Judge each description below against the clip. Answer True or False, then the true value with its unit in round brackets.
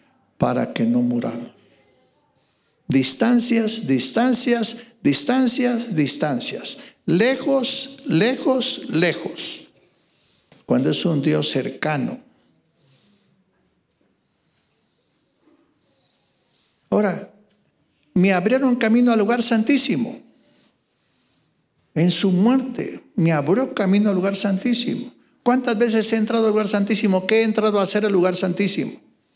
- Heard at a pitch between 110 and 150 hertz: False (230 Hz)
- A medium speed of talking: False (95 wpm)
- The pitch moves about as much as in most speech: True (4.0 semitones)